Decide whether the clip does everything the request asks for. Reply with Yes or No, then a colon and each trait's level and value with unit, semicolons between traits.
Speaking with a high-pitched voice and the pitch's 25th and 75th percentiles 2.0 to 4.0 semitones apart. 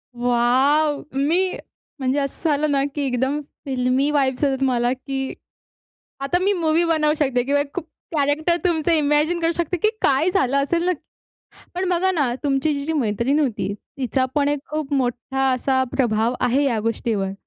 Yes: very high, 280 Hz; average, 3.3 semitones